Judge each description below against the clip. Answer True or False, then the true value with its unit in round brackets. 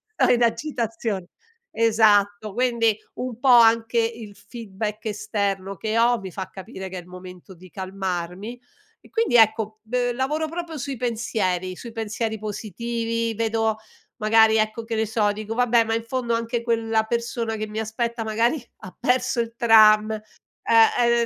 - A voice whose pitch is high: True (225 Hz)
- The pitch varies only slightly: True (1.9 semitones)